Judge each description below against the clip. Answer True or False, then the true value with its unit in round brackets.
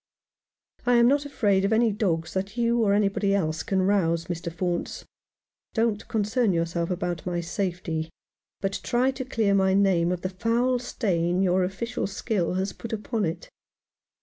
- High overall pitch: True (195 Hz)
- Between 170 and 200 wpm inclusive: True (175 wpm)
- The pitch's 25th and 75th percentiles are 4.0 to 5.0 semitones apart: True (4.3 semitones)